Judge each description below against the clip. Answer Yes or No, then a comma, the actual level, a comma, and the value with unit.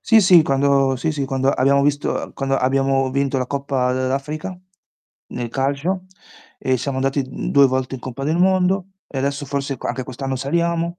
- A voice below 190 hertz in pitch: Yes, medium, 140 Hz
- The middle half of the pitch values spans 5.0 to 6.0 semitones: No, narrow, 2.4 semitones